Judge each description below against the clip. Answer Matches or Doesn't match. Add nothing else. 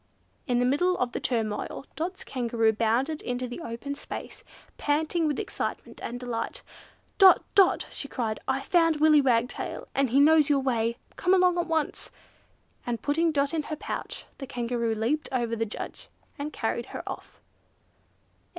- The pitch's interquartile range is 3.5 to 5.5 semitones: Matches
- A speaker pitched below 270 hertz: Doesn't match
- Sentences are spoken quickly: Doesn't match